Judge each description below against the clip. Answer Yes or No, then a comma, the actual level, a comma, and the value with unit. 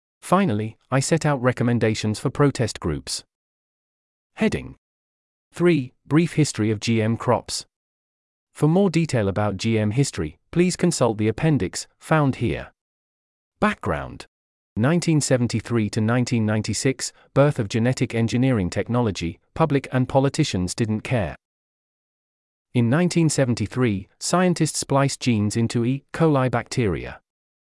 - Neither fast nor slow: No, slow, 110 wpm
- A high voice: No, low, 120 Hz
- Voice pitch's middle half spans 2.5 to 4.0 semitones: No, average, 5.0 semitones